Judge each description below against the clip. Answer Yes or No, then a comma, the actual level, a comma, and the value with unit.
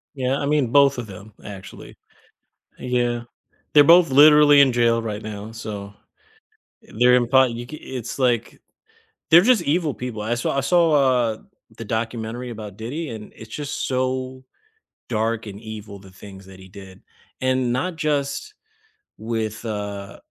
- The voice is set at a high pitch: No, low, 120 Hz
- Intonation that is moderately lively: Yes, average, 4.2 semitones